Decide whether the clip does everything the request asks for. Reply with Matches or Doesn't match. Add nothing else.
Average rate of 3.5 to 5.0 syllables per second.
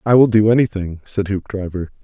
Doesn't match